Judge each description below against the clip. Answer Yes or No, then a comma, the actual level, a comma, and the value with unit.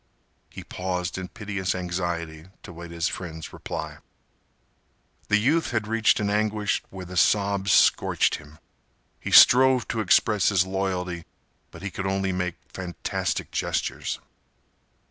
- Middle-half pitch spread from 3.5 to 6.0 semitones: No, average, 2.8 semitones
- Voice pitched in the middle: No, very low, 95 Hz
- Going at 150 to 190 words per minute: No, slow, 135 wpm